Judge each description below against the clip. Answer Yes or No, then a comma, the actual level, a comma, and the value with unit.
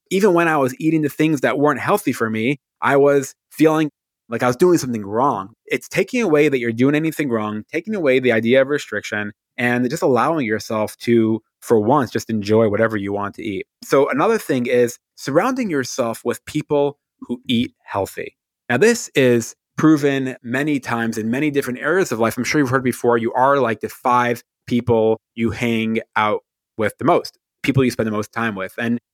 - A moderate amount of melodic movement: Yes, average, 4.5 semitones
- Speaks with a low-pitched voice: Yes, low, 125 Hz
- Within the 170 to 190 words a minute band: No, average, 200 wpm